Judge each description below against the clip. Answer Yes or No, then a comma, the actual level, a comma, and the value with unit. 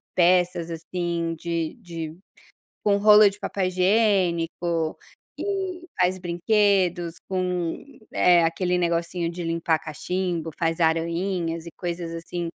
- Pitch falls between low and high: Yes, medium, 175 Hz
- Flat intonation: Yes, narrow, 1.8 semitones